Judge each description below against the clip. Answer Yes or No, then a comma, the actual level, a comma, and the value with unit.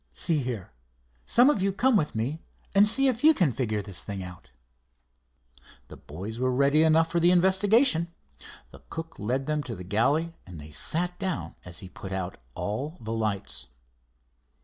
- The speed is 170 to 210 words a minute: Yes, average, 175 wpm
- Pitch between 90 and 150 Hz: Yes, medium, 140 Hz